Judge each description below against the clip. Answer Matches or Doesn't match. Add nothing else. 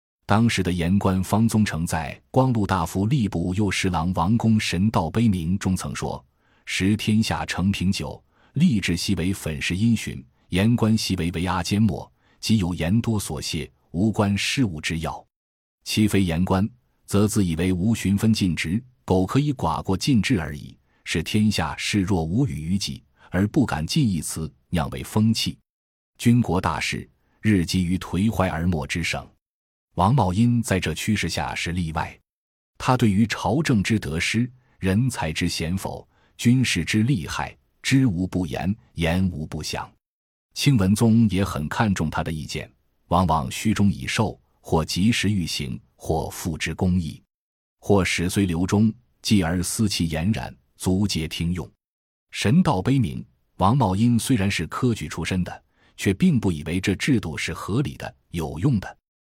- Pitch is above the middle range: Doesn't match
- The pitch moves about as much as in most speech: Matches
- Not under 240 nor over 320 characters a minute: Doesn't match